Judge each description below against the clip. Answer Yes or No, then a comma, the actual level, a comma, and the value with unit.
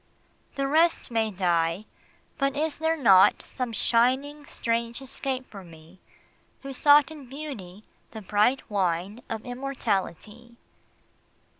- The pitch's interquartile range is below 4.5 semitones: No, wide, 5.5 semitones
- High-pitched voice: Yes, high, 235 Hz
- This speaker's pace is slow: Yes, slow, 120 wpm